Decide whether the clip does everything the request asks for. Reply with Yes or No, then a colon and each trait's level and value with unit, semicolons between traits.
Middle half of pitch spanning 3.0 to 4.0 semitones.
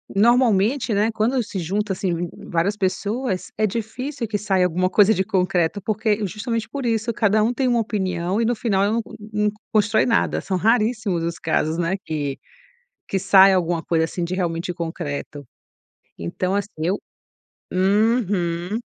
Yes: average, 3.7 semitones